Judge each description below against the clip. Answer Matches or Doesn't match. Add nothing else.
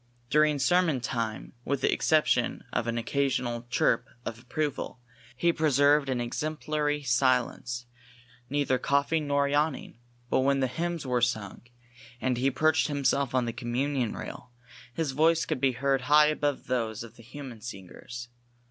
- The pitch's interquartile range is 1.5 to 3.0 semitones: Doesn't match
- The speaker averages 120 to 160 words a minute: Matches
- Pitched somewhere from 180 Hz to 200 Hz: Doesn't match